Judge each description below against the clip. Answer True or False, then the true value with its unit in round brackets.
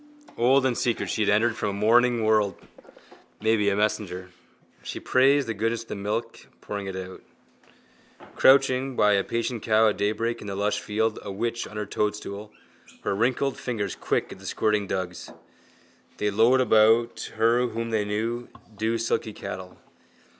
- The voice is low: True (110 Hz)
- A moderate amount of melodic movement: False (2.3 semitones)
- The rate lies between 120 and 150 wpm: False (165 wpm)